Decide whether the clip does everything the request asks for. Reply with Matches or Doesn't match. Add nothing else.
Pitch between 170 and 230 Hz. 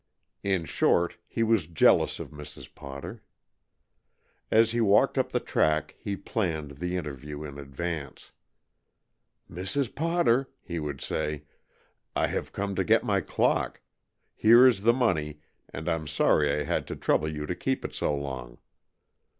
Doesn't match